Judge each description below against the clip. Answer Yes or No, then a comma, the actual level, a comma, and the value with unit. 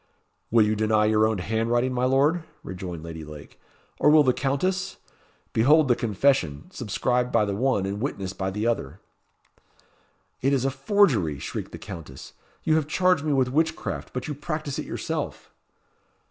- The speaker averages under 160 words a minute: No, average, 165 wpm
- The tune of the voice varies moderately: No, wide, 6.0 semitones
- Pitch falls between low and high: No, low, 125 Hz